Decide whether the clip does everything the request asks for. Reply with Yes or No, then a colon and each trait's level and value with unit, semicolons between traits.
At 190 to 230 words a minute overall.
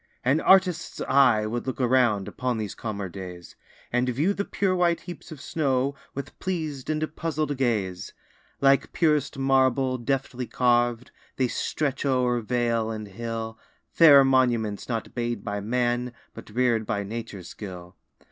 No: average, 145 wpm